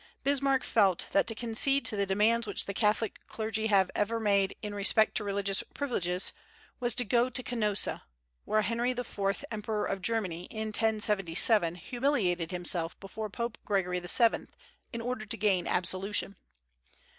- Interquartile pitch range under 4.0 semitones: Yes, average, 2.9 semitones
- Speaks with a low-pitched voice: No, high, 210 Hz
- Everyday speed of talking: Yes, average, 155 wpm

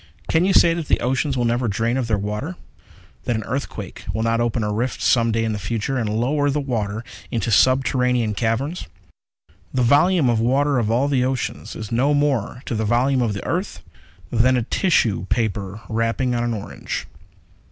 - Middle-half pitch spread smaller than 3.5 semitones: Yes, average, 3.1 semitones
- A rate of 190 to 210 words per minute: Yes, average, 195 wpm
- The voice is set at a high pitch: No, low, 120 Hz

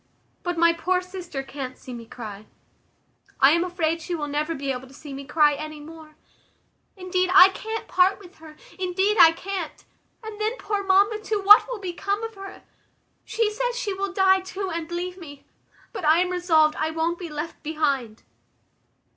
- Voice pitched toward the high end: Yes, very high, 345 Hz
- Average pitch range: Yes, average, 4.1 semitones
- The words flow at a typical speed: Yes, average, 185 wpm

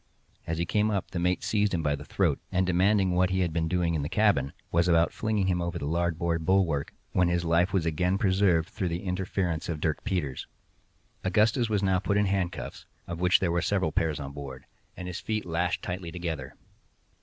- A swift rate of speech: Yes, fast, 215 wpm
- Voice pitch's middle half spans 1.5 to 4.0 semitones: Yes, narrow, 2.5 semitones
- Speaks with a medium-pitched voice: No, very low, 90 Hz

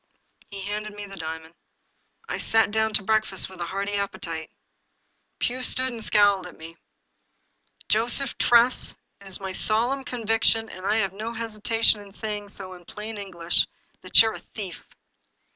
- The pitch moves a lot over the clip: No, average, 2.8 semitones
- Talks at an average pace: Yes, average, 165 wpm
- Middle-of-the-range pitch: No, high, 205 Hz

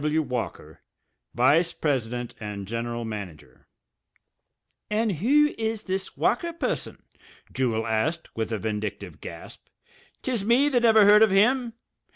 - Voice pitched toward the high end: No, medium, 155 Hz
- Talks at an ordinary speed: No, slow, 130 wpm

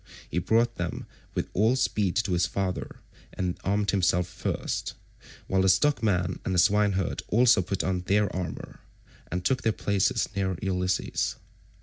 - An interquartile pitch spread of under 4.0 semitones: Yes, narrow, 2.5 semitones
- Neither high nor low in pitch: No, very low, 95 Hz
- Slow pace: No, average, 150 wpm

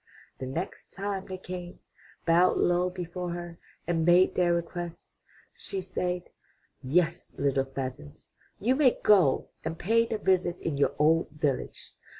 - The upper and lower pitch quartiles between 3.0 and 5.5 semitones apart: No, narrow, 2.5 semitones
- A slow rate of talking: No, average, 145 wpm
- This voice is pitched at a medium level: Yes, medium, 175 Hz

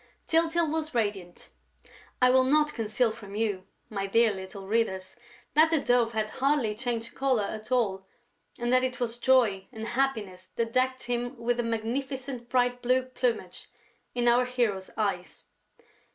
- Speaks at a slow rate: No, average, 155 wpm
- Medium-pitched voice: No, high, 240 Hz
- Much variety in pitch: No, average, 3.3 semitones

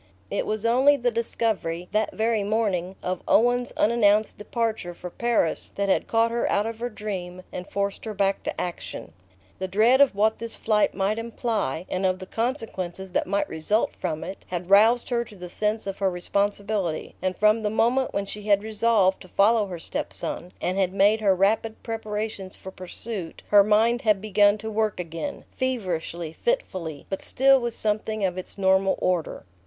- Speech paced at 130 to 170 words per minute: No, average, 185 wpm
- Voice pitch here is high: Yes, high, 205 Hz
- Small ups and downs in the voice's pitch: No, average, 3.2 semitones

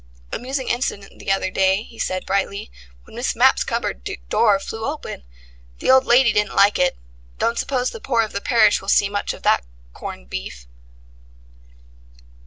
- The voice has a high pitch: Yes, high, 210 Hz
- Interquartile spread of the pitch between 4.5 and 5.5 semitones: No, average, 3.8 semitones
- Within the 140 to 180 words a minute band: Yes, average, 170 wpm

